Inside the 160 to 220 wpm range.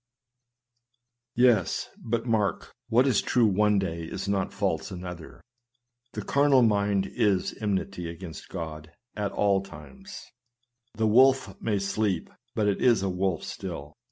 No: average, 150 wpm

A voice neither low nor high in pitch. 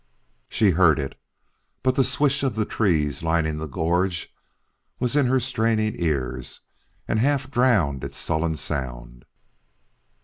No: very low, 90 Hz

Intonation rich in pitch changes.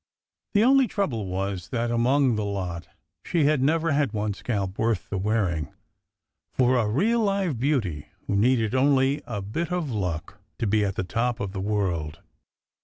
Yes: wide, 6.2 semitones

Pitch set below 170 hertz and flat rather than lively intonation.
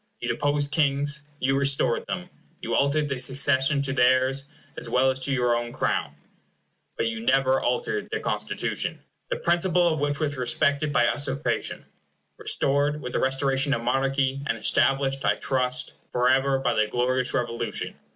Yes: low, 135 Hz; narrow, 2.1 semitones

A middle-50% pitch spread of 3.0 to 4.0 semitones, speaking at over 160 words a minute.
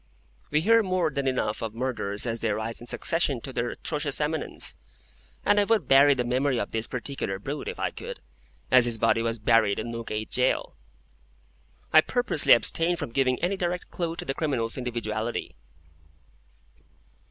No: average, 5.0 semitones; average, 170 wpm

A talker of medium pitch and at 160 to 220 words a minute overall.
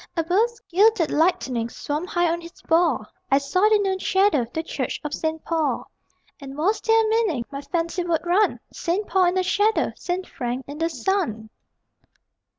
No: very high, 340 Hz; average, 175 wpm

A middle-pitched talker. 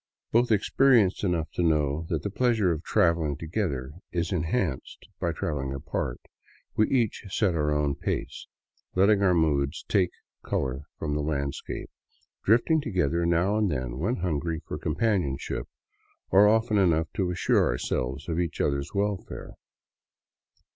No: very low, 85 Hz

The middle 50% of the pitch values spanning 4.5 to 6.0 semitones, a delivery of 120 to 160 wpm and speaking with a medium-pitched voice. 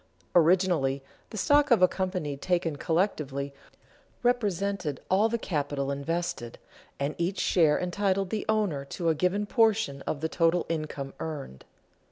Yes: wide, 5.6 semitones; average, 140 wpm; medium, 170 Hz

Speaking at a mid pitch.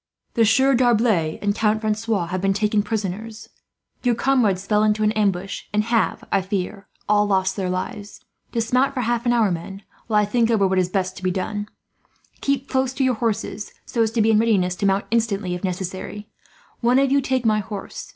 No: high, 210 Hz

